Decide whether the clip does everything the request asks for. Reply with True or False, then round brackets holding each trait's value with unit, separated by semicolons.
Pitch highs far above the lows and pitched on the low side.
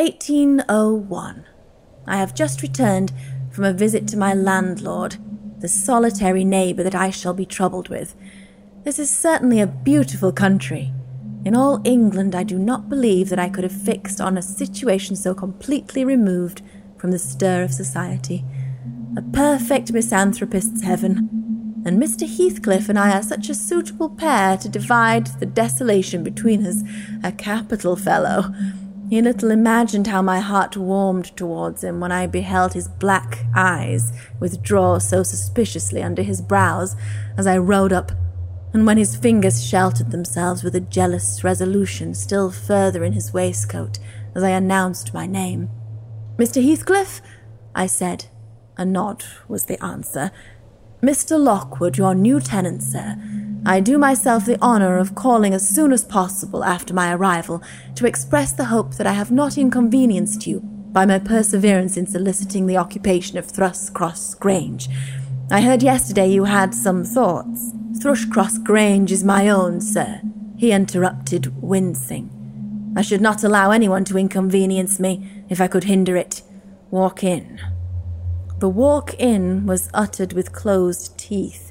False (8.0 semitones; 190 Hz)